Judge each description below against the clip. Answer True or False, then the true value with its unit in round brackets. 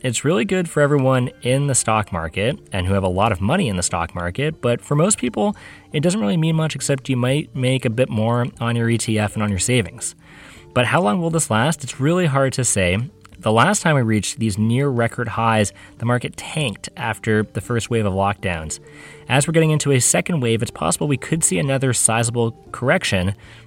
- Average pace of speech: False (220 wpm)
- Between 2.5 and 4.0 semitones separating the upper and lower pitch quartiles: False (4.9 semitones)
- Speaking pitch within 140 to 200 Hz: False (120 Hz)